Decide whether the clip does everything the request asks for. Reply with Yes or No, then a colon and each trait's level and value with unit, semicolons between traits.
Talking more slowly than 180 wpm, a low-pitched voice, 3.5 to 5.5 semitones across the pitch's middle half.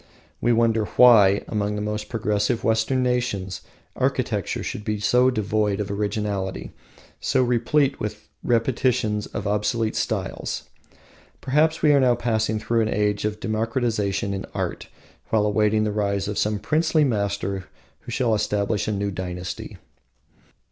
No: average, 140 wpm; low, 105 Hz; narrow, 2.5 semitones